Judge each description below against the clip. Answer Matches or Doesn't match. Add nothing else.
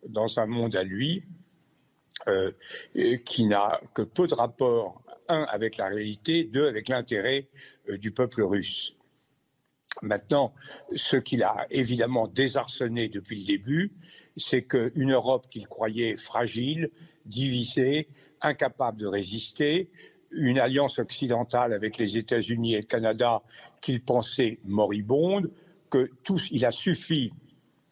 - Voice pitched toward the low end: Matches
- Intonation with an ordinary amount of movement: Doesn't match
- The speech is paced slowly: Matches